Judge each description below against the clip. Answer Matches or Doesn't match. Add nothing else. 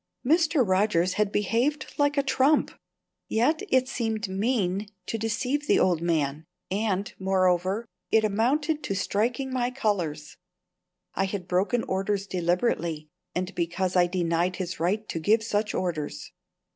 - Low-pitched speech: Doesn't match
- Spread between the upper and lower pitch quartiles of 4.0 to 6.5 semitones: Matches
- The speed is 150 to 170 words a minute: Doesn't match